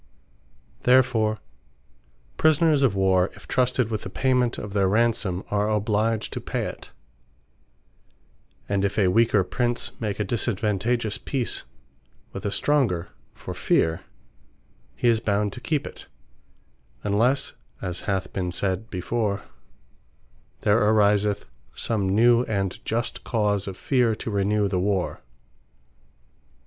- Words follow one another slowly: Yes, slow, 125 wpm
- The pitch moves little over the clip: No, average, 3.2 semitones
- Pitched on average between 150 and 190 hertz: No, low, 105 Hz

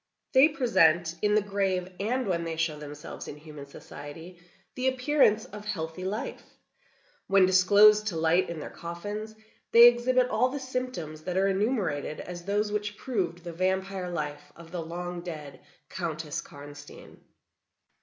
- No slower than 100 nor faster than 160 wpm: Yes, average, 155 wpm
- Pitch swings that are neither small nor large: Yes, average, 4.5 semitones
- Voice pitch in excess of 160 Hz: Yes, medium, 185 Hz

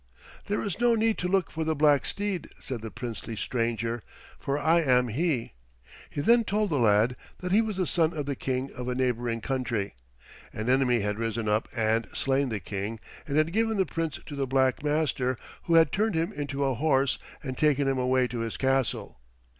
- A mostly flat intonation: No, average, 5.2 semitones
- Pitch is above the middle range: No, low, 135 Hz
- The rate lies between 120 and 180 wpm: No, fast, 205 wpm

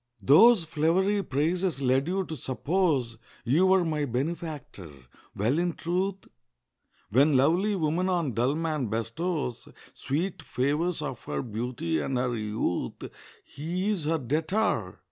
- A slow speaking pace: Yes, slow, 130 wpm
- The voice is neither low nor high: Yes, medium, 155 Hz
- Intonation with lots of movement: Yes, wide, 5.9 semitones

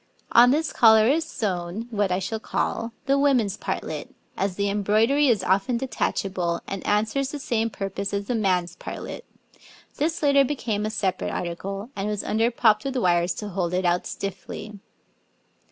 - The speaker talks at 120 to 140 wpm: No, average, 170 wpm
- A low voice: No, high, 210 Hz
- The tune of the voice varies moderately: Yes, average, 4.0 semitones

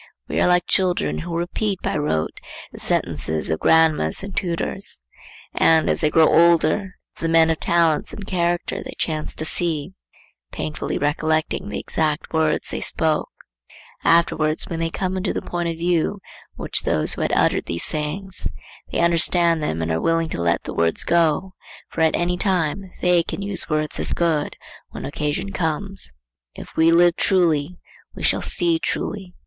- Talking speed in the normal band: Yes, average, 170 wpm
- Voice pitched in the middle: Yes, medium, 165 Hz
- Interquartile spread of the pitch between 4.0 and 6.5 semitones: No, narrow, 2.5 semitones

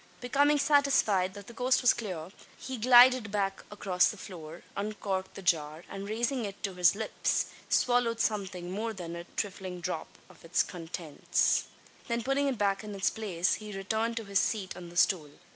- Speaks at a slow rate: No, average, 180 wpm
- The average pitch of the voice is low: No, high, 200 Hz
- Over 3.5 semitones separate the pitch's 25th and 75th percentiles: Yes, average, 4.3 semitones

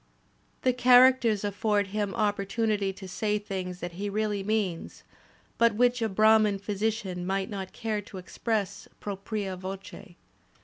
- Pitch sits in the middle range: No, high, 205 Hz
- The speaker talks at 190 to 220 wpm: No, average, 140 wpm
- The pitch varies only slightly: Yes, narrow, 2.2 semitones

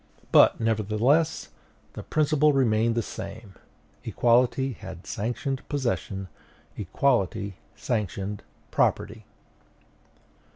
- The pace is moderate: No, slow, 80 wpm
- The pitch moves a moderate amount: Yes, average, 4.9 semitones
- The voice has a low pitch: Yes, low, 115 Hz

